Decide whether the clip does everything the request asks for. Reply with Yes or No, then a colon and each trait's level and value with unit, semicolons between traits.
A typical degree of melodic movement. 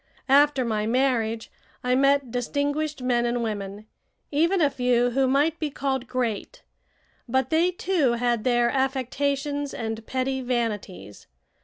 Yes: average, 3.1 semitones